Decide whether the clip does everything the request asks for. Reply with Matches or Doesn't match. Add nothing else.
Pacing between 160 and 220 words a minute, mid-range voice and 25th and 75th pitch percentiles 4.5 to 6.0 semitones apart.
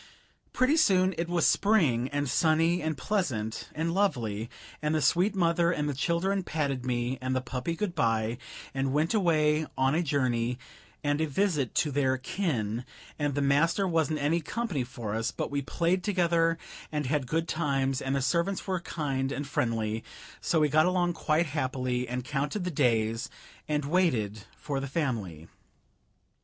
Matches